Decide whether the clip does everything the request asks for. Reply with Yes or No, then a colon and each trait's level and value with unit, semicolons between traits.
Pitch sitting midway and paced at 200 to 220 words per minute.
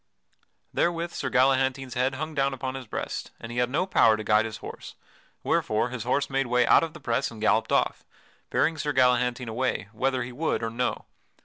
No: low, 125 Hz; fast, 205 wpm